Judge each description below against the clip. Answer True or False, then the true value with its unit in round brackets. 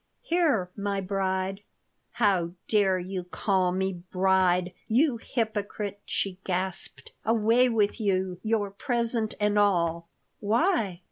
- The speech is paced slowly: True (115 wpm)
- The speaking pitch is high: True (200 Hz)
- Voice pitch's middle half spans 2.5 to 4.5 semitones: True (3.0 semitones)